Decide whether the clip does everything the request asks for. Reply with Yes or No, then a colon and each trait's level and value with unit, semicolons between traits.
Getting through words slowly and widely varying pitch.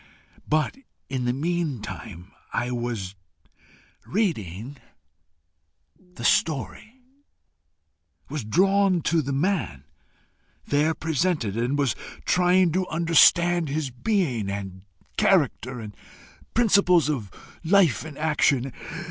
Yes: slow, 95 wpm; wide, 6.5 semitones